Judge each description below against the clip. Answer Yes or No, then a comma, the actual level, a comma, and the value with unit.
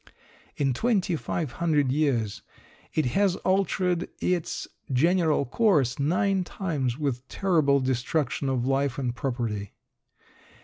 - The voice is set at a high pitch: No, medium, 145 Hz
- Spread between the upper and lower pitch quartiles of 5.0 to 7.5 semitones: Yes, wide, 5.5 semitones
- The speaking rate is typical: No, slow, 100 wpm